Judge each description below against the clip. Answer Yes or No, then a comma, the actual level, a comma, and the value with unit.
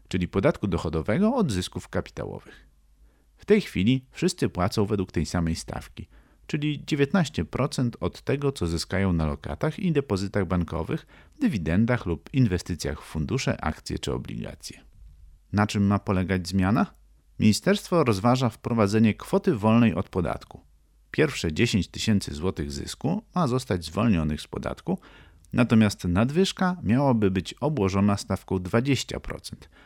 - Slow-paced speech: No, average, 125 wpm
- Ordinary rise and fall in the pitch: No, wide, 7.0 semitones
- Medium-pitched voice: No, low, 100 Hz